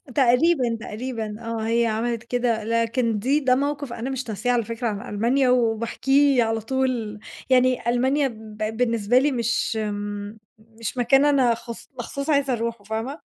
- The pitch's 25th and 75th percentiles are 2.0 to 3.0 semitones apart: Yes, average, 2.7 semitones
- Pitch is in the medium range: No, high, 235 Hz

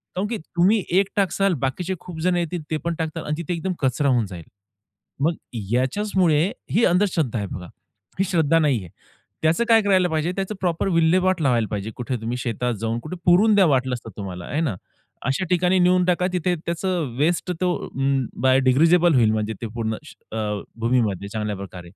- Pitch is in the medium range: Yes, medium, 160 Hz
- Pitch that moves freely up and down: Yes, wide, 6.7 semitones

